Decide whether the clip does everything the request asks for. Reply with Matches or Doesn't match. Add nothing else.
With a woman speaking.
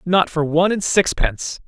Doesn't match